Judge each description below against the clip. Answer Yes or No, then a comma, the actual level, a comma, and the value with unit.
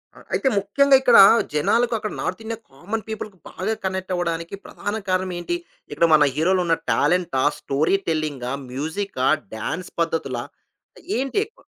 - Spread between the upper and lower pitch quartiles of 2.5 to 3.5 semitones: No, average, 4.8 semitones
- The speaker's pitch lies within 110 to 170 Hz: No, medium, 180 Hz